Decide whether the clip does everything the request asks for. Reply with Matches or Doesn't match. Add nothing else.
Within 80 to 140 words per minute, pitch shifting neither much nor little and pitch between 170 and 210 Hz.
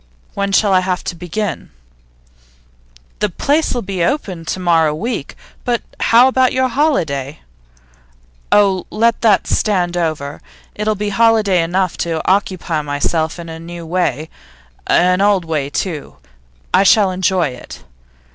Matches